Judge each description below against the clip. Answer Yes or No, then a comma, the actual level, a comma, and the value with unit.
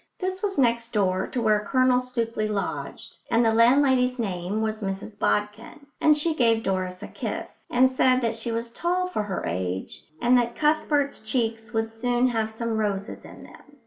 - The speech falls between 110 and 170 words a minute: No, average, 180 wpm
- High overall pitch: Yes, high, 230 Hz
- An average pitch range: Yes, average, 3.1 semitones